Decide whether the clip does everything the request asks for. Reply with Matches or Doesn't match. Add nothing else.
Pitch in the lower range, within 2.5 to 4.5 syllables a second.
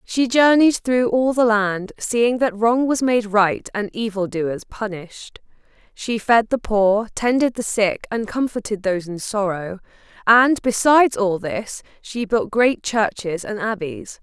Doesn't match